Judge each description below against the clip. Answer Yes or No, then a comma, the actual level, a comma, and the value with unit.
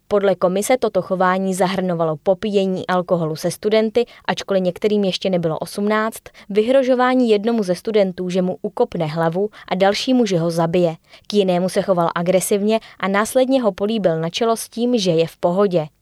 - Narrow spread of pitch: No, average, 3.3 semitones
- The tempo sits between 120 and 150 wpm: No, average, 165 wpm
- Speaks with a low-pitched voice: No, high, 190 Hz